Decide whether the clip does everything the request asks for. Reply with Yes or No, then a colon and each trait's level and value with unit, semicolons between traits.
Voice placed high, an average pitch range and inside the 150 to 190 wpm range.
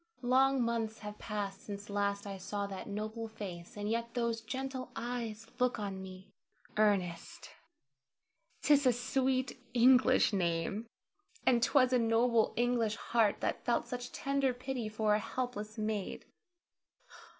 No: high, 225 Hz; average, 3.3 semitones; average, 140 wpm